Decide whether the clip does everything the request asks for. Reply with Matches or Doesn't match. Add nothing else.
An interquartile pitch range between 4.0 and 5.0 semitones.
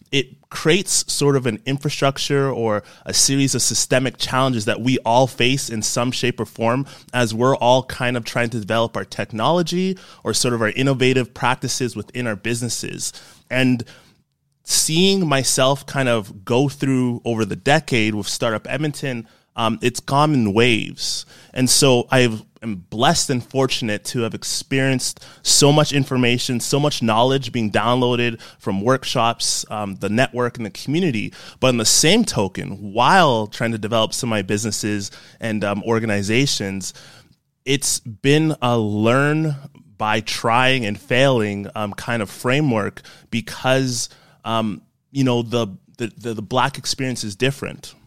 Doesn't match